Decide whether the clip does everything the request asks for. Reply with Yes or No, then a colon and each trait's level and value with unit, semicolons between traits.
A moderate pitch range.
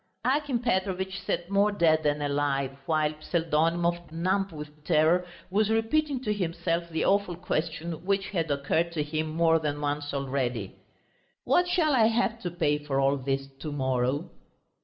Yes: average, 4.7 semitones